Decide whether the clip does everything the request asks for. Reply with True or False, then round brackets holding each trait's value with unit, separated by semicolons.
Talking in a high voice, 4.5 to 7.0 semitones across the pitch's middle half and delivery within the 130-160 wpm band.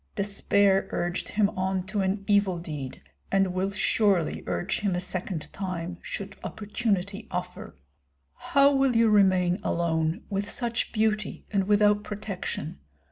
False (195 Hz; 2.6 semitones; 135 wpm)